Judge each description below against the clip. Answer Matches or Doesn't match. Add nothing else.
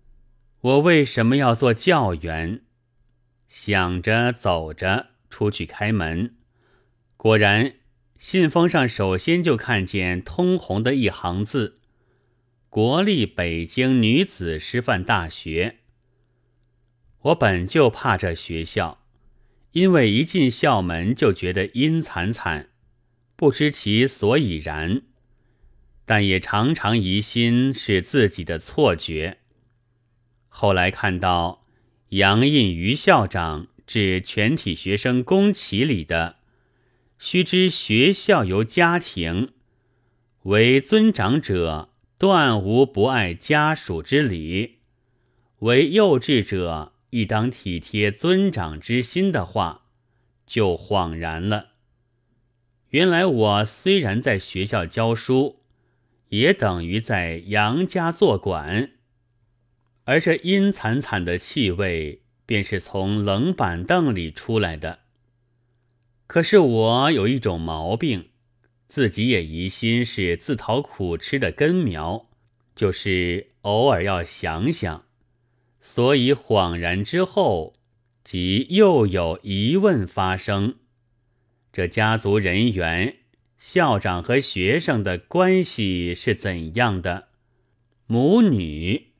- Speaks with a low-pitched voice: Matches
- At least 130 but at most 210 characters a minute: Matches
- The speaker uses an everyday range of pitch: Matches